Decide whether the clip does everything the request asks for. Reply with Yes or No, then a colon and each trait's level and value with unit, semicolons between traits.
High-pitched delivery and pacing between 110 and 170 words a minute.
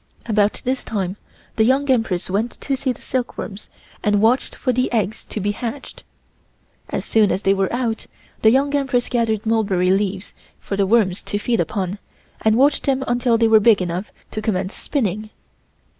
No: high, 220 Hz; average, 185 wpm